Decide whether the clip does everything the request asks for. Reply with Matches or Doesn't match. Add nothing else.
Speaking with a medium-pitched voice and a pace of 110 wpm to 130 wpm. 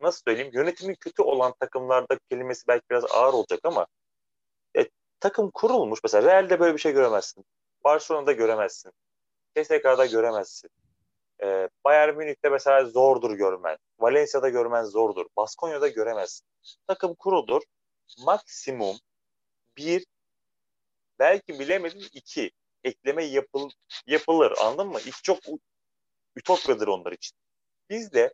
Matches